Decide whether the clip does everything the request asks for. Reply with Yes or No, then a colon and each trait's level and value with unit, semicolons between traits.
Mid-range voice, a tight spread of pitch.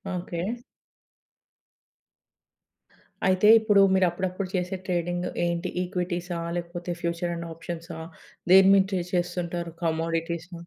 Yes: medium, 175 Hz; narrow, 1.3 semitones